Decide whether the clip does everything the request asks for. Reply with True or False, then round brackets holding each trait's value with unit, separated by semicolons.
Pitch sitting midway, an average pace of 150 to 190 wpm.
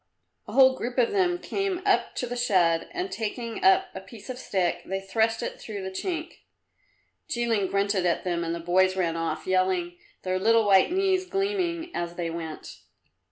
False (210 Hz; 185 wpm)